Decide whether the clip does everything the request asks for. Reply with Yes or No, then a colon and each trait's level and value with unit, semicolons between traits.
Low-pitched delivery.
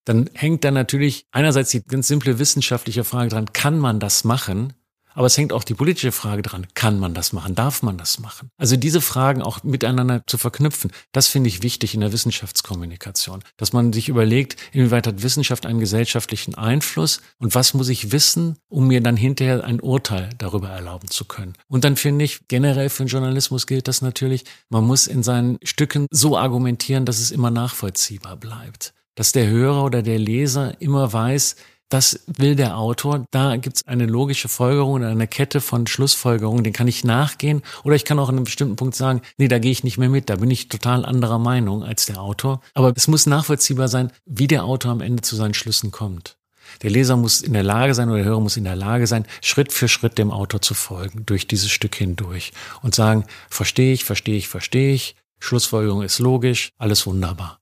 Yes: low, 125 Hz